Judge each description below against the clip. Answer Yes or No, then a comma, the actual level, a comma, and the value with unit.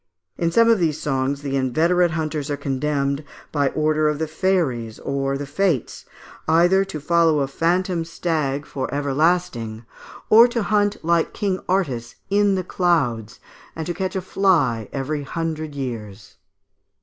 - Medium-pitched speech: Yes, medium, 155 Hz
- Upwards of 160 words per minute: No, average, 155 wpm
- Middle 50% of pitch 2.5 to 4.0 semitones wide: No, average, 4.5 semitones